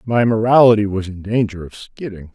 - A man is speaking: Yes, male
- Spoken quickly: No, average, 180 wpm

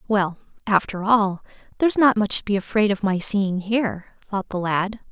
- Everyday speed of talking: Yes, average, 190 wpm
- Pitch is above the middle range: Yes, high, 205 Hz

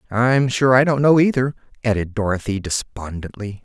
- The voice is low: Yes, low, 120 Hz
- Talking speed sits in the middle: Yes, average, 150 wpm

